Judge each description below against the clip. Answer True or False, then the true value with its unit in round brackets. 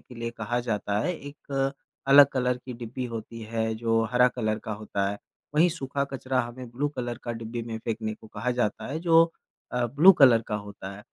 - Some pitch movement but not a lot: True (3.1 semitones)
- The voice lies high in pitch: False (120 Hz)